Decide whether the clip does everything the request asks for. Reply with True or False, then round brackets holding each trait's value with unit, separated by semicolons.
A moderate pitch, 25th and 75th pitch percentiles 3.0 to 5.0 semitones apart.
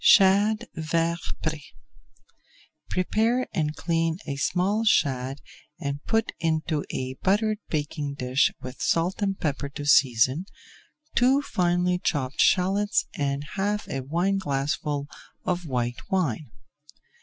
False (165 Hz; 5.4 semitones)